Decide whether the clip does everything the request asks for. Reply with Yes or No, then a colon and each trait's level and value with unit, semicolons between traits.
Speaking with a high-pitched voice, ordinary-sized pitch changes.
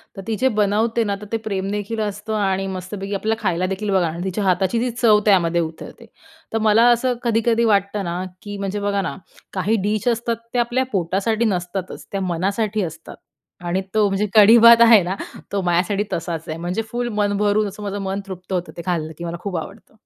Yes: high, 200 Hz; average, 3.0 semitones